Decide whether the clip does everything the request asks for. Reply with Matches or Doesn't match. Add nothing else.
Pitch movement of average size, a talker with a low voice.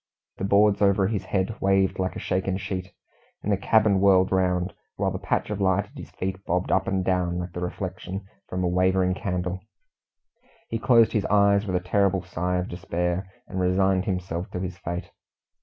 Doesn't match